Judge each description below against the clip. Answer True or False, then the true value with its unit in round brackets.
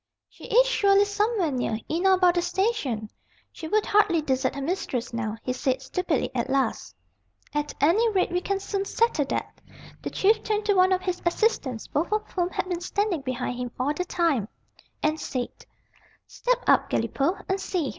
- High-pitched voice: True (355 Hz)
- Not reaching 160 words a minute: False (185 wpm)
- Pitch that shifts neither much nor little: False (6.7 semitones)